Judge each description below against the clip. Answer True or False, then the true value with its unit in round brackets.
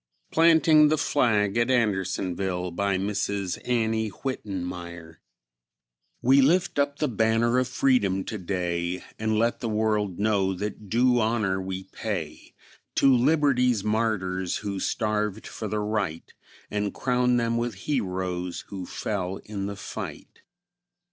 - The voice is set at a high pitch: False (105 Hz)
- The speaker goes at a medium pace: False (130 wpm)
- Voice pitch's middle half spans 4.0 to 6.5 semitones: True (4.3 semitones)